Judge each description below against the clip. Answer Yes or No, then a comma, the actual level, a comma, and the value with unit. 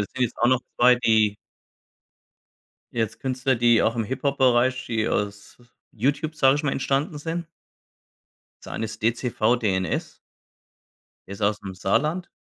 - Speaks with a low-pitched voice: Yes, low, 120 Hz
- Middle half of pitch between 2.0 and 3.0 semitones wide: No, average, 3.8 semitones